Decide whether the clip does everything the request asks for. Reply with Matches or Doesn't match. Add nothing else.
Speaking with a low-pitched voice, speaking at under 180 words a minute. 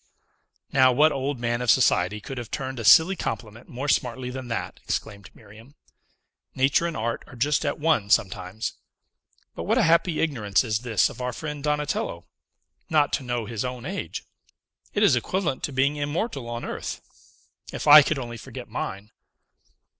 Matches